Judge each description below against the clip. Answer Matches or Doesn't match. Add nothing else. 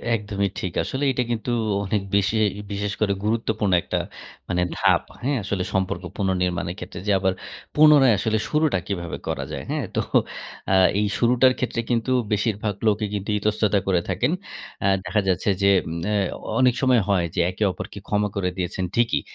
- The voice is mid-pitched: Doesn't match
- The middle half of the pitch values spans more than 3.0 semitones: Matches